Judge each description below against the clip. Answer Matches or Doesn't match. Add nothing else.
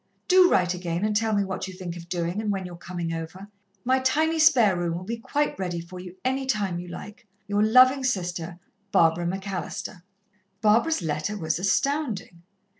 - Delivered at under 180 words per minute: Doesn't match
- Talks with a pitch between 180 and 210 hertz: Matches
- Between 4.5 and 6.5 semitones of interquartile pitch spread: Matches